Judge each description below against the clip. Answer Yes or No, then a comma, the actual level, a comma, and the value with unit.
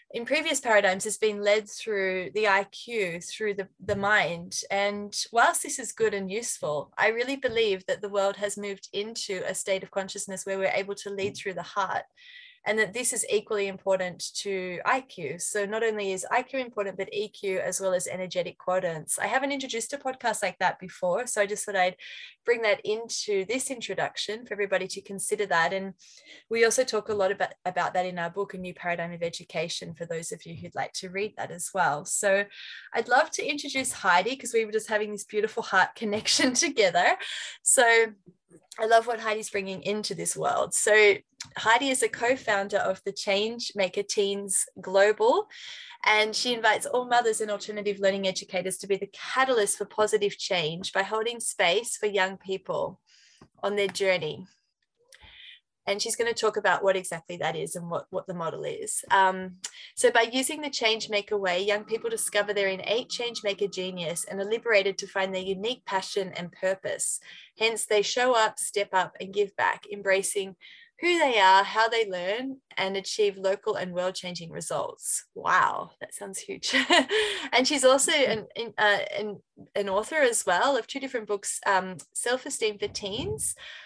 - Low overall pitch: No, high, 205 Hz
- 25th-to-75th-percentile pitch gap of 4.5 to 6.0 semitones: No, average, 3.5 semitones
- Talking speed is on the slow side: No, average, 185 wpm